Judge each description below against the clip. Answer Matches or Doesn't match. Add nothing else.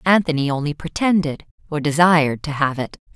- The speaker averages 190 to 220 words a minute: Doesn't match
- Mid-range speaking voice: Matches